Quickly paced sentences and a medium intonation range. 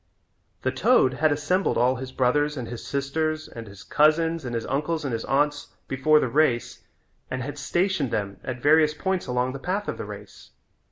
No: average, 190 wpm; average, 3.7 semitones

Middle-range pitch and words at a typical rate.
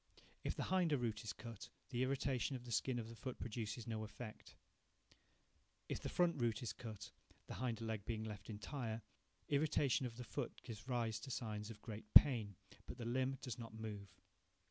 No: low, 115 Hz; average, 185 wpm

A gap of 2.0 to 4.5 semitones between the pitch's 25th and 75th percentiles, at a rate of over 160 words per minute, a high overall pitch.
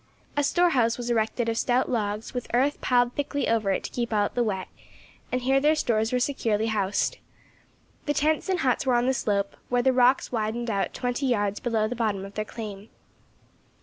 Yes: average, 3.0 semitones; average, 200 wpm; high, 240 Hz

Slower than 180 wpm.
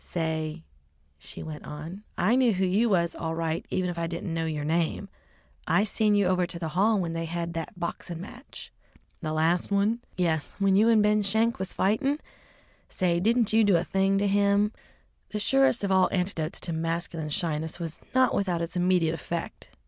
No: average, 195 wpm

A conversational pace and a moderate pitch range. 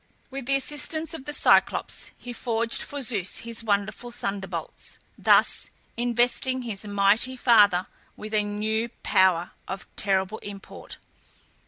No: slow, 130 wpm; average, 3.7 semitones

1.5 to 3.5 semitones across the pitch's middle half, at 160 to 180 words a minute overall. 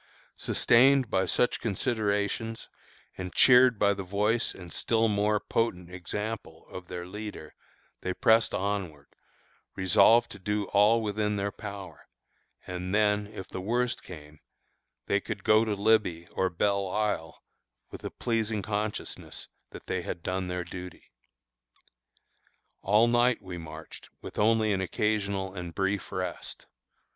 No: average, 2.9 semitones; slow, 135 wpm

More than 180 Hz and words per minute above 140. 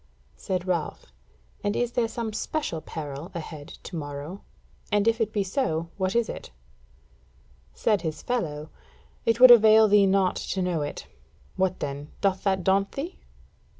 Yes: high, 190 Hz; average, 155 wpm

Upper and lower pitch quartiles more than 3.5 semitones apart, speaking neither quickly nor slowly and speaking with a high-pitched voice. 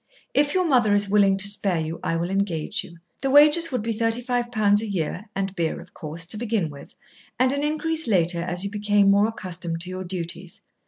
No: average, 5.0 semitones; fast, 220 wpm; high, 200 Hz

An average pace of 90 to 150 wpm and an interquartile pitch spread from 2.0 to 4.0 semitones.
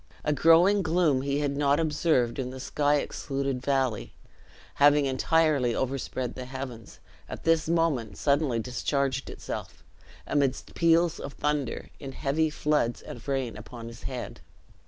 Yes: average, 140 wpm; average, 2.9 semitones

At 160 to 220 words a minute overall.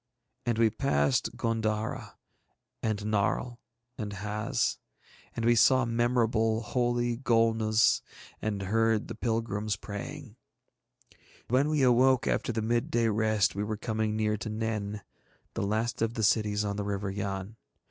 No: slow, 135 wpm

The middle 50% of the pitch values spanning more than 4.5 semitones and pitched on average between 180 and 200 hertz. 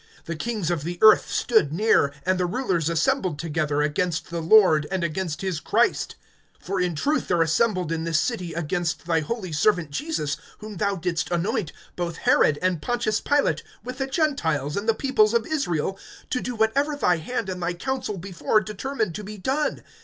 Yes: average, 5.2 semitones; medium, 185 Hz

